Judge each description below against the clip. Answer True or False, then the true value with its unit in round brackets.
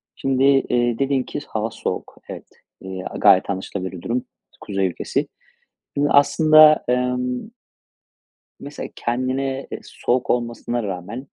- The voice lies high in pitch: False (125 Hz)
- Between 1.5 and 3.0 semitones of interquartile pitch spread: False (4.5 semitones)